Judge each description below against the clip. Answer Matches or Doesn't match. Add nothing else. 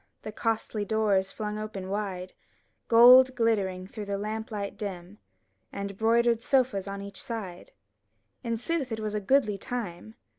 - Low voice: Doesn't match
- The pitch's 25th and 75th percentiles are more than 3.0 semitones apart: Doesn't match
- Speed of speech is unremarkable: Matches